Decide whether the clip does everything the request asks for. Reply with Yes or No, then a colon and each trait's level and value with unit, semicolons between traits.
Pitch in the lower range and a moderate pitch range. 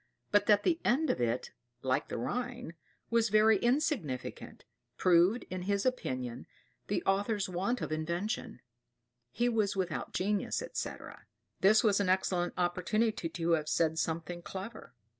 No: high, 195 Hz; average, 4.7 semitones